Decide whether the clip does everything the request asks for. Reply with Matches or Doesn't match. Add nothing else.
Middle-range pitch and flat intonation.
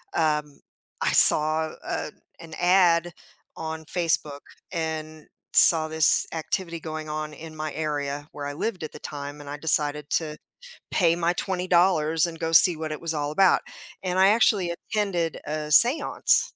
Matches